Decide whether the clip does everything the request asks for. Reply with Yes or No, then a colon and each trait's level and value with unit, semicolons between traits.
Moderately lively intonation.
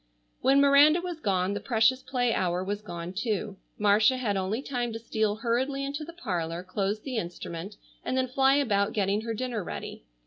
Yes: average, 4.8 semitones